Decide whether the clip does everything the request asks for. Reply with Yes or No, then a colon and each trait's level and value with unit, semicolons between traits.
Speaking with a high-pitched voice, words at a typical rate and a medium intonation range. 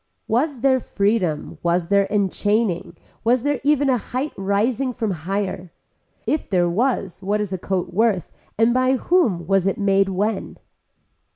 Yes: high, 205 Hz; average, 155 wpm; average, 4.7 semitones